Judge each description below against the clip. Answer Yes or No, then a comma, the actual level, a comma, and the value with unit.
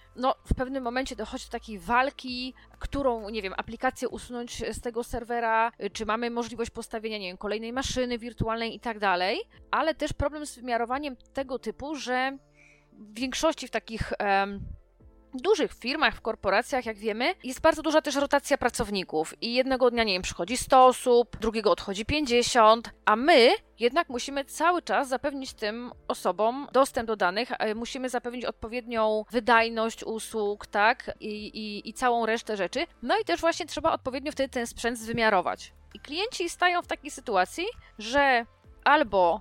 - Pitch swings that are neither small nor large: Yes, average, 3.6 semitones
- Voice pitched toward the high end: Yes, high, 240 Hz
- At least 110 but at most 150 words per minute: No, fast, 160 wpm